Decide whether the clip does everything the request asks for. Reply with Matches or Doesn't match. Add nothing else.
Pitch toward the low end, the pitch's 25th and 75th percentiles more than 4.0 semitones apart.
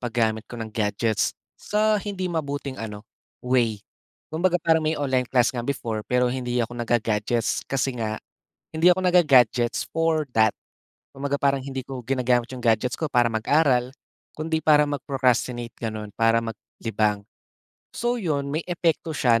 Matches